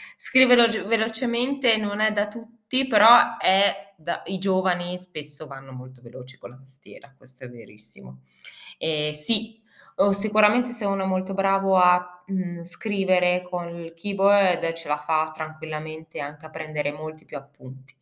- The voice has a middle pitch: Yes, medium, 180 Hz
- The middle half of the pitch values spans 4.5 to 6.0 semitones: Yes, average, 5.2 semitones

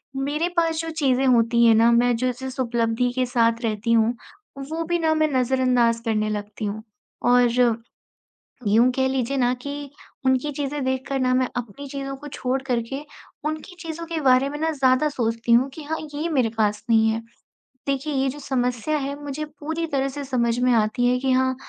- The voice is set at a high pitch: Yes, very high, 255 Hz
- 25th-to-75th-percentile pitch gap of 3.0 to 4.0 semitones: Yes, average, 3.3 semitones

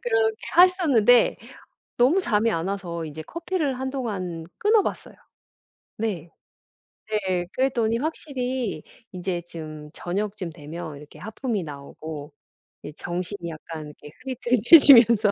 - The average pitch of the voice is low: No, high, 210 Hz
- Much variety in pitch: Yes, wide, 7.5 semitones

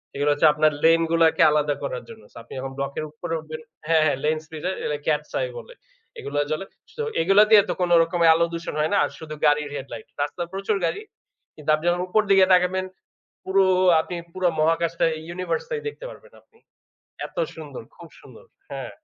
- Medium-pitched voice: Yes, medium, 165 Hz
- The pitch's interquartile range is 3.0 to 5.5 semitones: Yes, average, 3.5 semitones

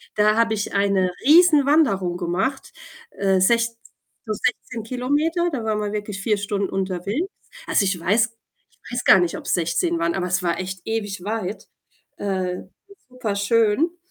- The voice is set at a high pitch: Yes, high, 210 Hz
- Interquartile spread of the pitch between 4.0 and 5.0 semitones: Yes, average, 4.5 semitones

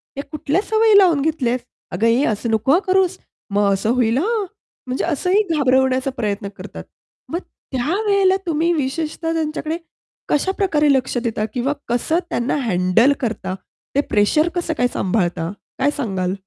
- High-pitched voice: Yes, very high, 275 Hz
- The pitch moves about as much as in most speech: No, wide, 6.2 semitones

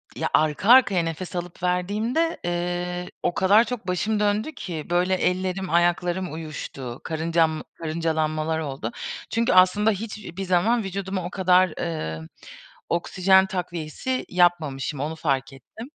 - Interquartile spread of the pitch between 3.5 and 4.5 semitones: No, average, 3.1 semitones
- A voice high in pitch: No, medium, 180 Hz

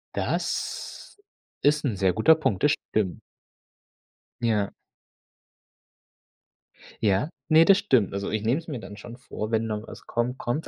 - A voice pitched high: No, low, 115 Hz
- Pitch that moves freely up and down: Yes, wide, 5.8 semitones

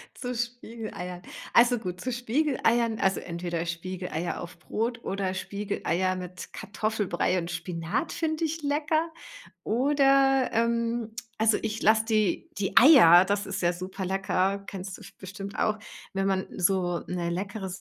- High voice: Yes, high, 200 Hz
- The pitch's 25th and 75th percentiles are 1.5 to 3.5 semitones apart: No, average, 4.5 semitones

